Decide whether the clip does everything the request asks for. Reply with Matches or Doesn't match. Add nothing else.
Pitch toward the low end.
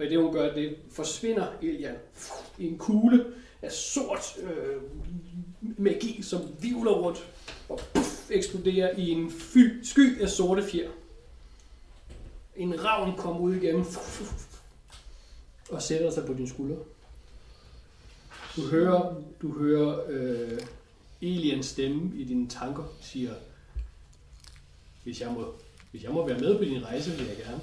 Doesn't match